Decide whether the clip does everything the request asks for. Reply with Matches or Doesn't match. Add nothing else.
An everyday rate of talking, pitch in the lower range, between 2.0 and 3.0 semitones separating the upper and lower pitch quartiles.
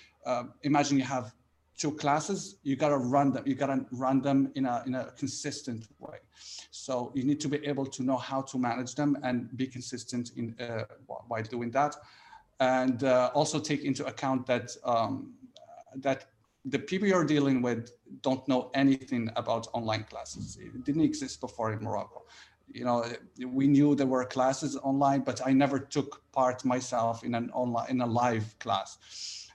Matches